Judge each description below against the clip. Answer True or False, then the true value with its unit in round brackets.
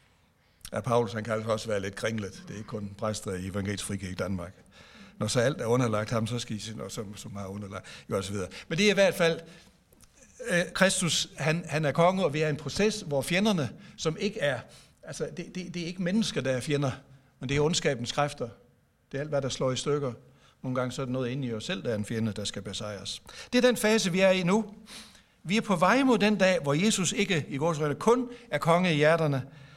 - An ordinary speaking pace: False (245 wpm)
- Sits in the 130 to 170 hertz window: True (140 Hz)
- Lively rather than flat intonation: True (8.4 semitones)